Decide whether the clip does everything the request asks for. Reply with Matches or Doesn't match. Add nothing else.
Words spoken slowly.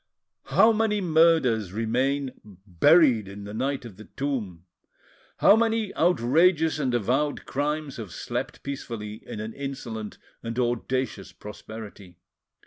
Matches